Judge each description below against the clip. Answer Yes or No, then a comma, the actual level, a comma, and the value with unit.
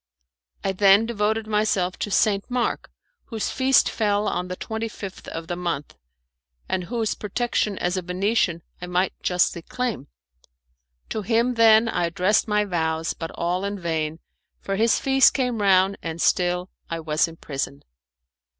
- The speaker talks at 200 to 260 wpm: No, average, 160 wpm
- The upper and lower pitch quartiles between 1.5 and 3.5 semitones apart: No, average, 3.9 semitones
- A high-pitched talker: Yes, high, 195 Hz